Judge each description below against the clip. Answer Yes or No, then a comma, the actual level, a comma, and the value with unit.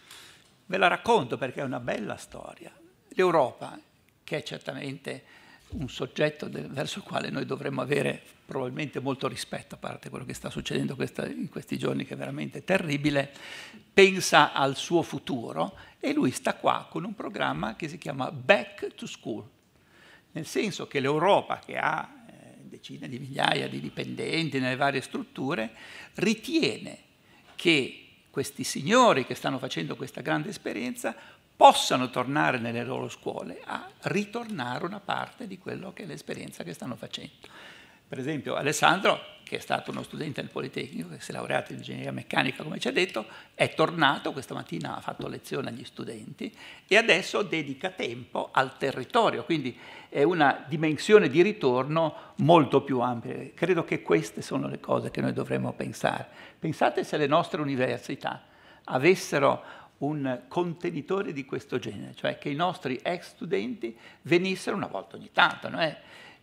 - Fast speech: No, average, 155 wpm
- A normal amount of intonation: No, wide, 5.7 semitones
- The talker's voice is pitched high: No, medium, 140 Hz